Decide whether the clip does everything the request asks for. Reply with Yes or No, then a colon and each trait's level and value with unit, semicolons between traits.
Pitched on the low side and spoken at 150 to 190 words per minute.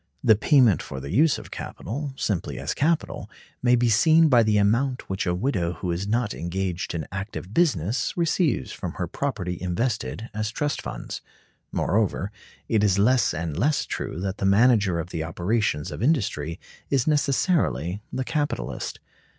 Yes: low, 105 Hz; average, 165 wpm